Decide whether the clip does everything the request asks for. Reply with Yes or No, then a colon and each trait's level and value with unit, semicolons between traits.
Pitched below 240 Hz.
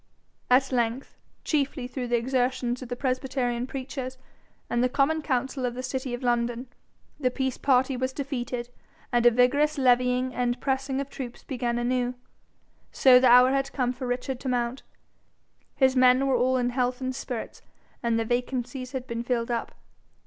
No: very high, 255 Hz